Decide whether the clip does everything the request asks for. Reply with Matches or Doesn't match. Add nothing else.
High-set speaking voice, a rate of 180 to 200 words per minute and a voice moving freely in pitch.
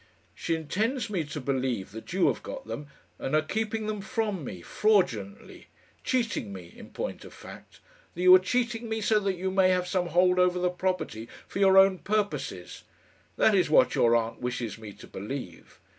Doesn't match